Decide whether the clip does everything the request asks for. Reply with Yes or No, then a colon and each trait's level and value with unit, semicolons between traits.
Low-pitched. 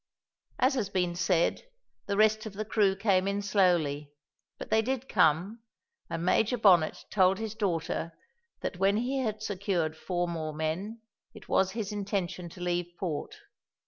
No: high, 195 Hz